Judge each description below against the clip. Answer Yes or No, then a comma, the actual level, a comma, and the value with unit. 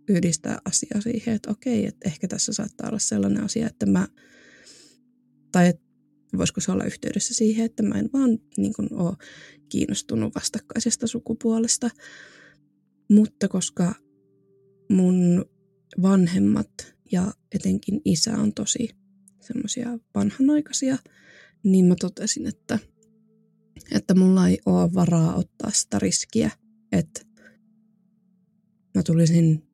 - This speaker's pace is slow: No, average, 115 wpm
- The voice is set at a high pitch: Yes, high, 205 Hz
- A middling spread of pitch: Yes, average, 4.0 semitones